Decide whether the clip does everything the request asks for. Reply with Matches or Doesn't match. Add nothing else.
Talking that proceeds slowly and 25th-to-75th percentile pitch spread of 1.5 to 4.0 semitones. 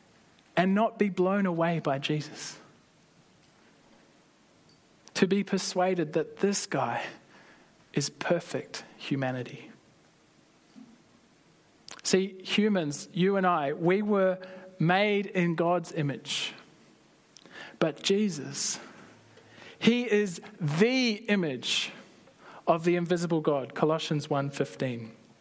Doesn't match